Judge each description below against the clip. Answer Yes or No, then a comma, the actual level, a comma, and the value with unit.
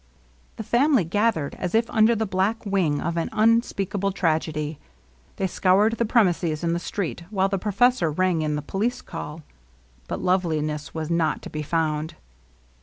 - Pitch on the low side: No, medium, 185 Hz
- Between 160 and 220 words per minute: Yes, average, 170 wpm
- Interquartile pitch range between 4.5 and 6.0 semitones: Yes, average, 4.9 semitones